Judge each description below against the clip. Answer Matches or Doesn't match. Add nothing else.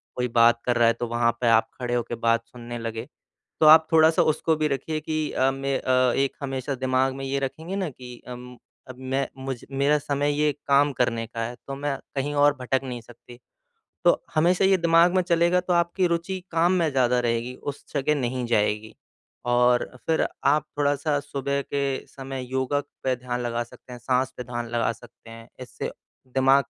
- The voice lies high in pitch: Doesn't match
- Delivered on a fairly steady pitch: Doesn't match